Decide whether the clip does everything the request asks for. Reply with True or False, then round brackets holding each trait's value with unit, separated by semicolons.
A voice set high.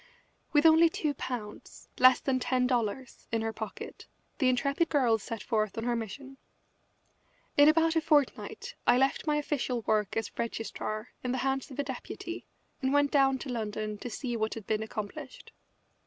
True (250 Hz)